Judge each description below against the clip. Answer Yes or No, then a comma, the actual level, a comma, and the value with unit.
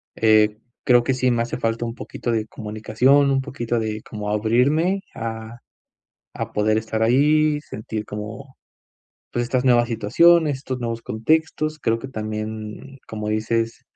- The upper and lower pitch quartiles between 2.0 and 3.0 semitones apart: No, average, 3.5 semitones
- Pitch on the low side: Yes, low, 115 Hz